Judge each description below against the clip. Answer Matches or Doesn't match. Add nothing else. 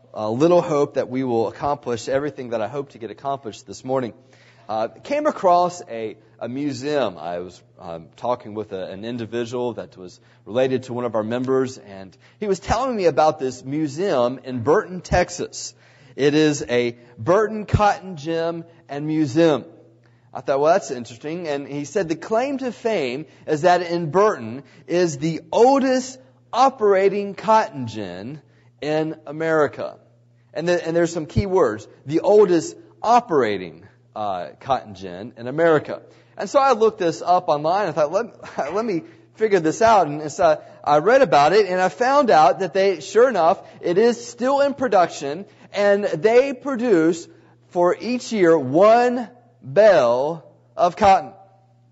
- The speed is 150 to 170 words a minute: Matches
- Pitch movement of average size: Doesn't match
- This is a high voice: Doesn't match